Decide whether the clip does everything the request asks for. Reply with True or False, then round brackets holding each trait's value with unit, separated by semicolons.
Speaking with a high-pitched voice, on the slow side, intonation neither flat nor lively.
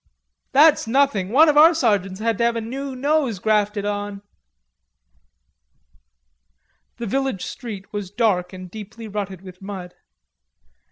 True (215 Hz; 130 wpm; 4.8 semitones)